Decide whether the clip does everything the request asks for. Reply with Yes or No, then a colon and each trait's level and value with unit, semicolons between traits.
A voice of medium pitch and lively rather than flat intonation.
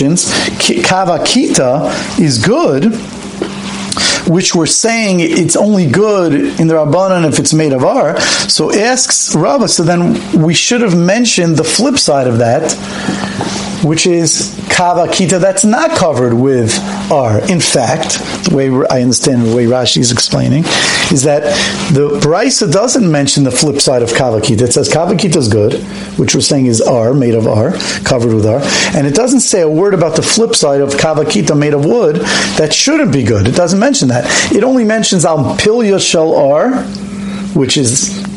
Yes: medium, 165 Hz; wide, 6.4 semitones